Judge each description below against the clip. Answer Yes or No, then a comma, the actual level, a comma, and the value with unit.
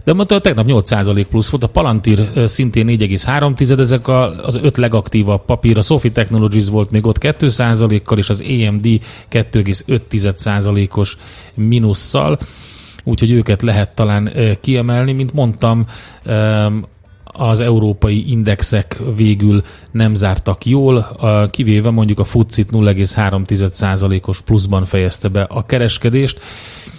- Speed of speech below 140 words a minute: Yes, average, 115 wpm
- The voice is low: Yes, low, 110 Hz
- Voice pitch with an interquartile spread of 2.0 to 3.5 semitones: Yes, narrow, 2.6 semitones